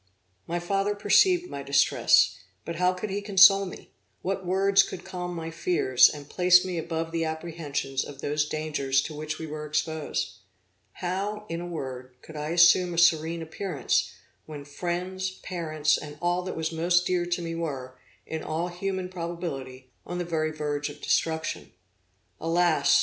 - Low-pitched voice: No, medium, 165 Hz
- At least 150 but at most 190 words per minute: Yes, average, 165 wpm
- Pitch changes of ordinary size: Yes, average, 3.0 semitones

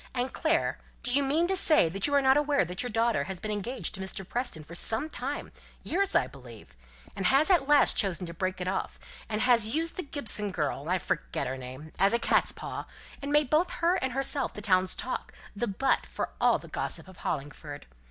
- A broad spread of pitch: Yes, wide, 7.5 semitones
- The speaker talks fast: Yes, fast, 220 wpm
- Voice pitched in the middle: No, high, 225 Hz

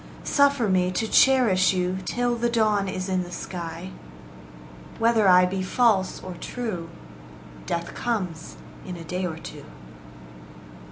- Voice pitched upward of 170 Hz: Yes, medium, 185 Hz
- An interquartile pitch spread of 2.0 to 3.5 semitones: No, average, 4.2 semitones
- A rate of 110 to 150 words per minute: Yes, slow, 135 wpm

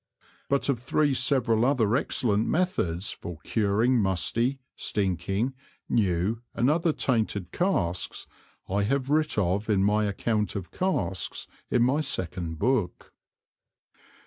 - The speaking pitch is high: No, low, 110 Hz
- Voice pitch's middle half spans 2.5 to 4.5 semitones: No, wide, 5.4 semitones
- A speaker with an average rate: No, slow, 120 wpm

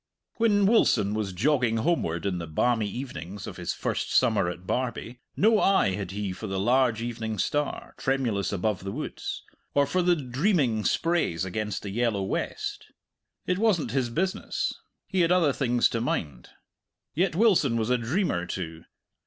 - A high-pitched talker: No, low, 120 Hz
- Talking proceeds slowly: No, average, 165 wpm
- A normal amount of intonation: No, wide, 7.6 semitones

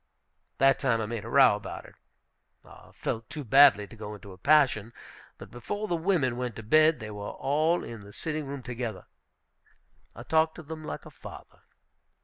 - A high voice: No, low, 125 Hz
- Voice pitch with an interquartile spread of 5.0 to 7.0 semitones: Yes, wide, 5.6 semitones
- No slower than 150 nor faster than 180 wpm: No, average, 190 wpm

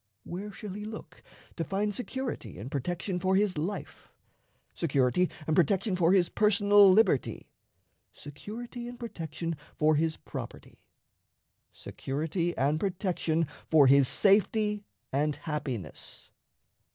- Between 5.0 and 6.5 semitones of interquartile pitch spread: Yes, average, 5.3 semitones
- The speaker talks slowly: Yes, slow, 115 wpm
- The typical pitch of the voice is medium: Yes, medium, 180 Hz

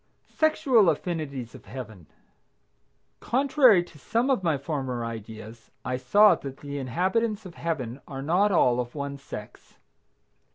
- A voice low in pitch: No, medium, 145 Hz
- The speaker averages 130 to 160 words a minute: Yes, slow, 135 wpm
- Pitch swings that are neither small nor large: No, wide, 7.9 semitones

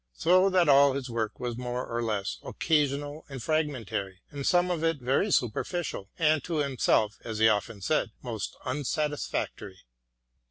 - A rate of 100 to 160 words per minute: Yes, average, 155 wpm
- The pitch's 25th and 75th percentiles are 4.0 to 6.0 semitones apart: Yes, wide, 5.4 semitones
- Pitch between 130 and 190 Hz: Yes, low, 135 Hz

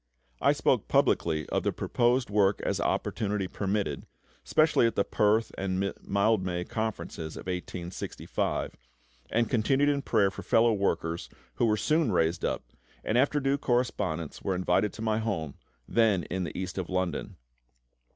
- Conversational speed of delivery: Yes, average, 150 wpm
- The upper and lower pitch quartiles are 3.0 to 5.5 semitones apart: Yes, average, 4.1 semitones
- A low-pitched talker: Yes, low, 100 Hz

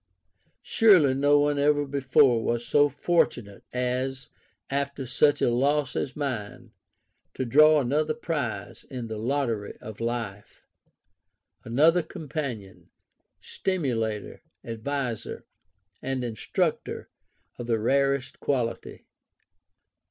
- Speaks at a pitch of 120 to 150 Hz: Yes, low, 135 Hz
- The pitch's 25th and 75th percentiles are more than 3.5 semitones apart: Yes, average, 3.9 semitones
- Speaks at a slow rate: Yes, slow, 105 wpm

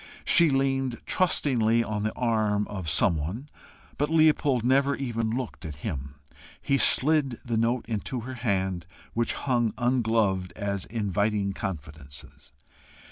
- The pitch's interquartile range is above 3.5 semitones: Yes, average, 4.8 semitones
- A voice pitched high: No, low, 115 Hz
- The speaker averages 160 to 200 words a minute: No, slow, 135 wpm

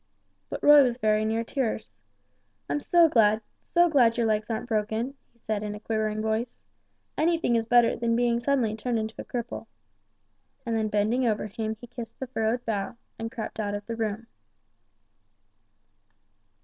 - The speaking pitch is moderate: No, high, 225 Hz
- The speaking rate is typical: Yes, average, 170 wpm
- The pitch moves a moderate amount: No, narrow, 2.0 semitones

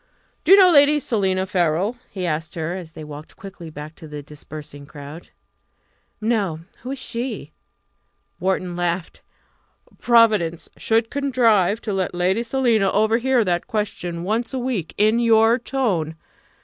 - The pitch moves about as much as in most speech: No, wide, 5.7 semitones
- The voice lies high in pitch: Yes, high, 195 Hz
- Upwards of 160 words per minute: No, average, 145 wpm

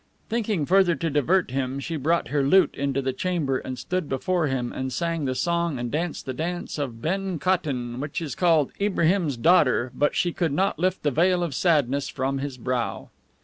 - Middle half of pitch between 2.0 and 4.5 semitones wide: No, average, 4.9 semitones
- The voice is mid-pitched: Yes, medium, 150 Hz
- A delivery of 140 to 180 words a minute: No, average, 195 wpm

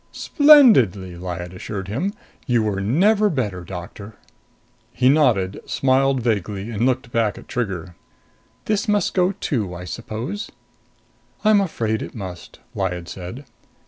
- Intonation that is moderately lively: No, wide, 7.2 semitones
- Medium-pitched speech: No, low, 115 Hz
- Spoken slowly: Yes, slow, 130 wpm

